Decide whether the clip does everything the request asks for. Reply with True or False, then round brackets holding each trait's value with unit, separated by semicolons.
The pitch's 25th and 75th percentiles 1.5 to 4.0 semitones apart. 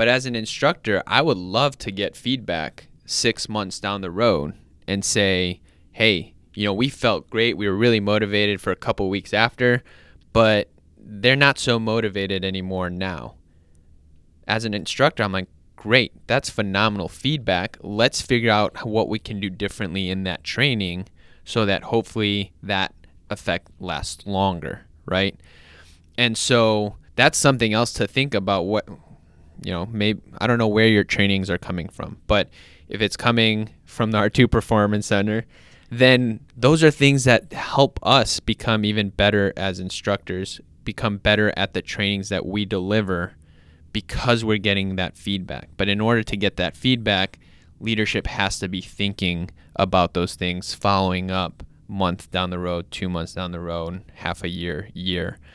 True (3.6 semitones)